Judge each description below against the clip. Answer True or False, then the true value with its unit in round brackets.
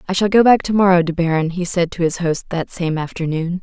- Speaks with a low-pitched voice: False (175 Hz)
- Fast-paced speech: True (265 wpm)